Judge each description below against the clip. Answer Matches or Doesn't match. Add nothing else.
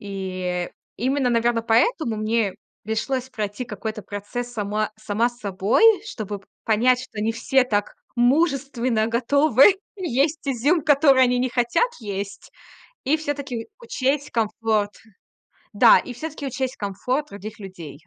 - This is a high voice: Matches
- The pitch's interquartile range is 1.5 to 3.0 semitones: Doesn't match